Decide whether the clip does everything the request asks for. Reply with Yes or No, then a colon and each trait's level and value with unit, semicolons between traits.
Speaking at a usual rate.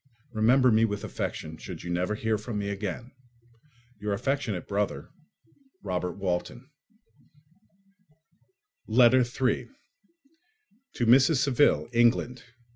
No: slow, 105 wpm